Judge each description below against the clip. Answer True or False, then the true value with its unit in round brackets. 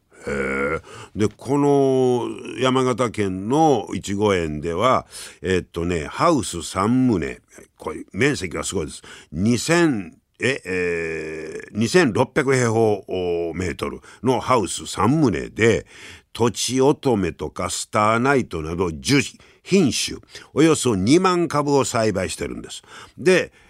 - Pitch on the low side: True (105 Hz)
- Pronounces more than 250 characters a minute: False (210 characters per minute)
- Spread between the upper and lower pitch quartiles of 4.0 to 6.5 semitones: False (6.9 semitones)